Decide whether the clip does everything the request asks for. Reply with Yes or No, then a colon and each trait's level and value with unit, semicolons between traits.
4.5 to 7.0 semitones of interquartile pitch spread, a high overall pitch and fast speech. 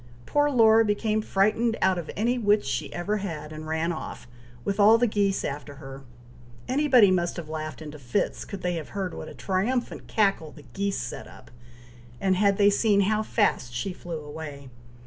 No: average, 5.2 semitones; high, 195 Hz; average, 185 wpm